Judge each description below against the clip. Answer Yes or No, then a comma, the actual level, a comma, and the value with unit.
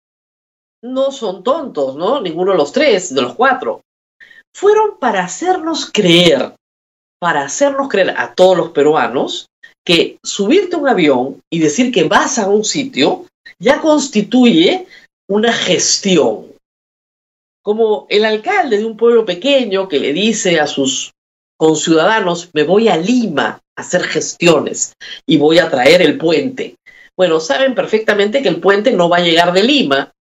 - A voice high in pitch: Yes, high, 215 Hz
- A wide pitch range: Yes, wide, 8.2 semitones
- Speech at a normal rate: Yes, average, 150 wpm